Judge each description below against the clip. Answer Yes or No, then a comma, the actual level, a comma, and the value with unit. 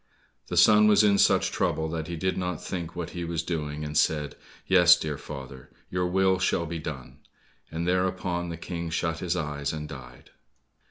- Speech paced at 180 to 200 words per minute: Yes, average, 185 wpm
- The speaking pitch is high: No, very low, 85 Hz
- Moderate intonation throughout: Yes, average, 3.0 semitones